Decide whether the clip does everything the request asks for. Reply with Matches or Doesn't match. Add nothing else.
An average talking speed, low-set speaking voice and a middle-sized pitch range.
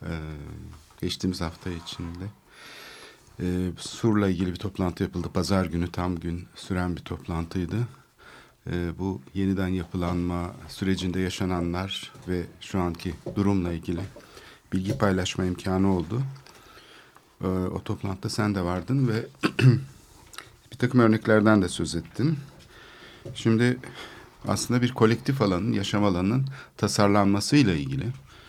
Matches